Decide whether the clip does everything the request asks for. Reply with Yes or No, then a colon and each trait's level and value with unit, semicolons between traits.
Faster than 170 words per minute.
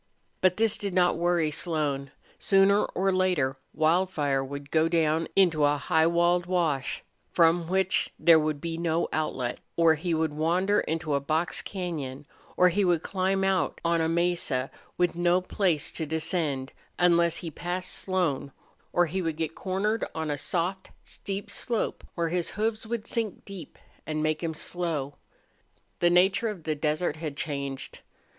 No: average, 165 wpm